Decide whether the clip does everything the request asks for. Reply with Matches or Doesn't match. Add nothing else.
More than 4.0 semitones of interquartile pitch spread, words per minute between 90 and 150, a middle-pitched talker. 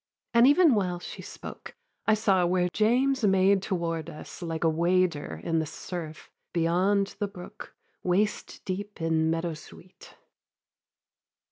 Doesn't match